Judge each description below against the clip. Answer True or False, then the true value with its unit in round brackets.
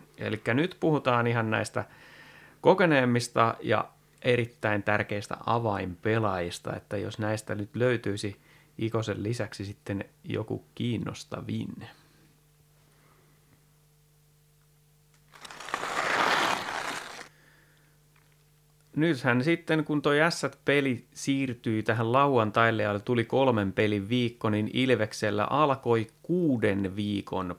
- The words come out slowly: True (85 wpm)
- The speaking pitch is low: True (120 Hz)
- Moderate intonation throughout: False (5.7 semitones)